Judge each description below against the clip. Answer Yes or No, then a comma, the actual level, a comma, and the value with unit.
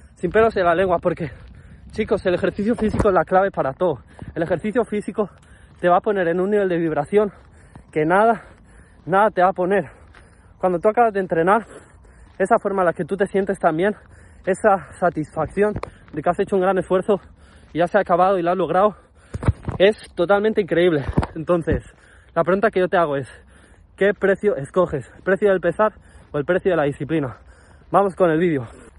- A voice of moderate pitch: Yes, medium, 180 Hz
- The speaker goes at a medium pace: No, fast, 195 wpm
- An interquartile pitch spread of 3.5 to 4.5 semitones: Yes, average, 3.8 semitones